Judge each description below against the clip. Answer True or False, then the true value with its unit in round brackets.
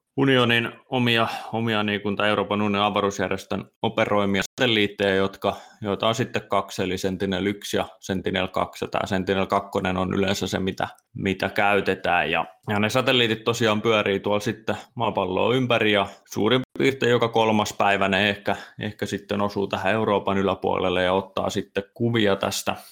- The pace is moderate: True (140 wpm)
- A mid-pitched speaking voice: False (100 Hz)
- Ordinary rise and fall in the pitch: False (2.3 semitones)